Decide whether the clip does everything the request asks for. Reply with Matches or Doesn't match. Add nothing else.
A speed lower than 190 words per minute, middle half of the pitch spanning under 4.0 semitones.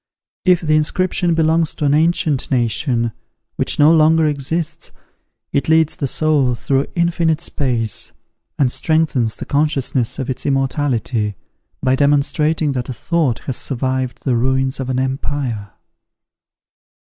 Matches